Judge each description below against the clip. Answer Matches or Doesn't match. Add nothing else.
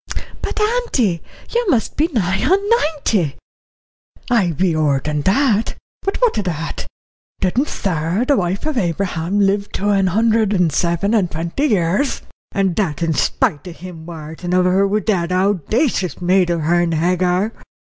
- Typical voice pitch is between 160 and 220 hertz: Matches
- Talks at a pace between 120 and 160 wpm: Matches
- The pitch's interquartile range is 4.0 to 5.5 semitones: Matches